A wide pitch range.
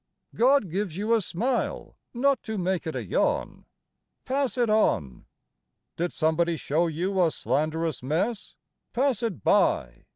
Yes: wide, 6.5 semitones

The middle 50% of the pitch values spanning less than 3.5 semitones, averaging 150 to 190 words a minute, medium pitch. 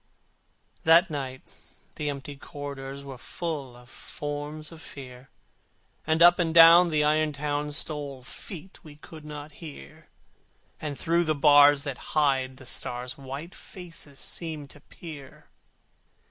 No: narrow, 2.5 semitones; slow, 135 wpm; medium, 145 Hz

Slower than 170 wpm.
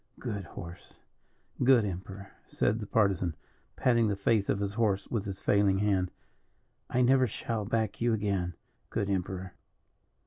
Yes: average, 145 wpm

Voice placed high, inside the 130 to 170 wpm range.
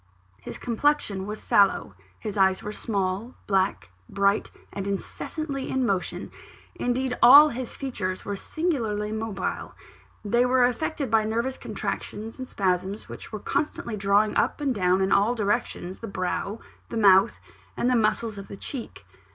Yes: high, 215 Hz; average, 150 wpm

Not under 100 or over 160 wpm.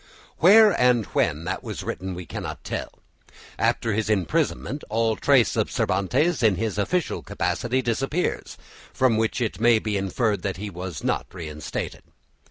Yes: average, 155 wpm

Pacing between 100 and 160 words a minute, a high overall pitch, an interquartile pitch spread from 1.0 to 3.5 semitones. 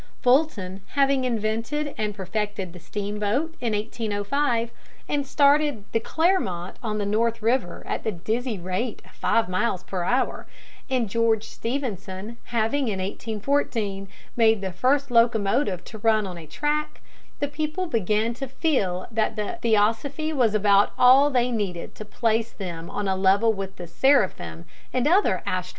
No: average, 155 wpm; high, 225 Hz; average, 4.5 semitones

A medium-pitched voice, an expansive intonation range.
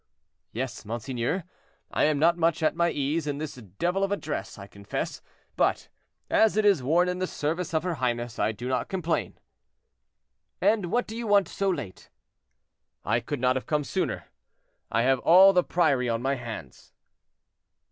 Yes: medium, 150 Hz; wide, 6.4 semitones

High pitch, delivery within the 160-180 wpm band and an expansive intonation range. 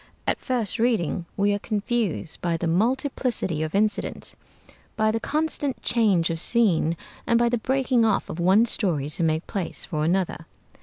Yes: high, 205 Hz; average, 165 wpm; wide, 5.9 semitones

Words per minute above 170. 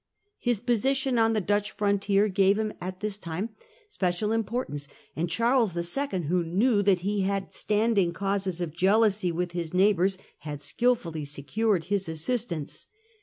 No: average, 150 wpm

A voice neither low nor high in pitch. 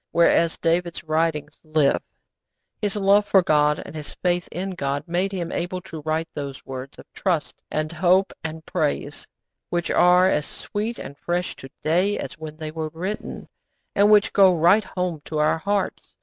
Yes: medium, 170 Hz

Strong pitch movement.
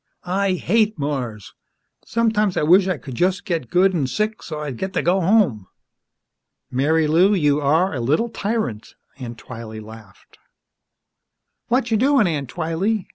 Yes: wide, 6.8 semitones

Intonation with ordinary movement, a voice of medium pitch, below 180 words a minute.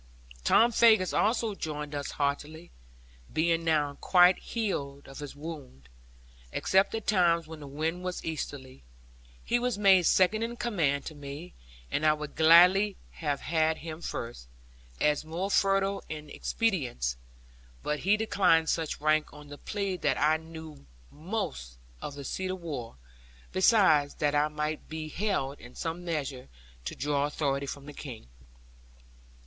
Yes: average, 4.4 semitones; medium, 155 Hz; average, 150 wpm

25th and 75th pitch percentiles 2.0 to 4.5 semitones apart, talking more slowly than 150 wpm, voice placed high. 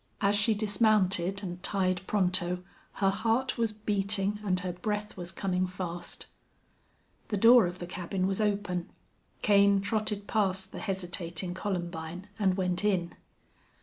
Yes: narrow, 2.4 semitones; average, 140 wpm; high, 195 Hz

